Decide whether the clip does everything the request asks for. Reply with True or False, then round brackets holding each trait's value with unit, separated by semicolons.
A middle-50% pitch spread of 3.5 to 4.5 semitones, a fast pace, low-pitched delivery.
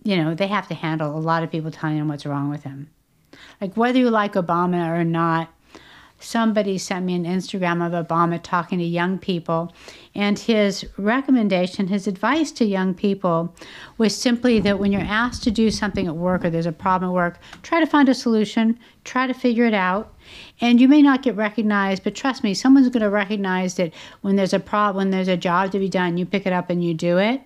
False (4.1 semitones; 225 wpm; 195 Hz)